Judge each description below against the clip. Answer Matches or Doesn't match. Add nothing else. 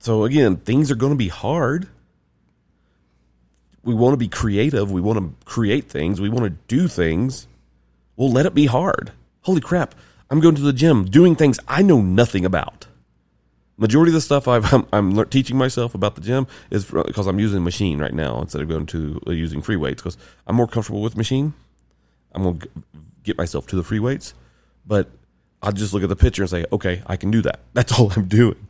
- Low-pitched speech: Matches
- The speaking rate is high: Matches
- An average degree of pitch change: Doesn't match